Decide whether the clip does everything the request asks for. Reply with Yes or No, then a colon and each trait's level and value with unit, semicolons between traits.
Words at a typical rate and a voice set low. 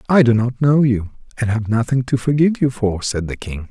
No: fast, 245 wpm; low, 120 Hz